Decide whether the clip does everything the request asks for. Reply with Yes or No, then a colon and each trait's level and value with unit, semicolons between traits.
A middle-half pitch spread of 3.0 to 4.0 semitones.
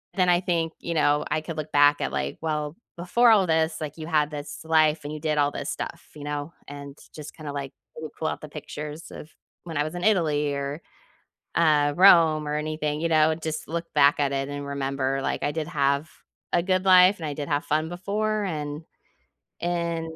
No: narrow, 2.4 semitones